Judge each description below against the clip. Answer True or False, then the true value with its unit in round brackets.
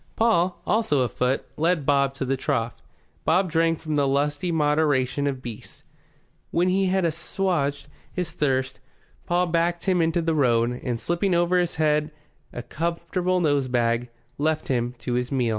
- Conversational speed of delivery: True (160 wpm)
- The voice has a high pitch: False (150 Hz)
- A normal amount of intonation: True (4.6 semitones)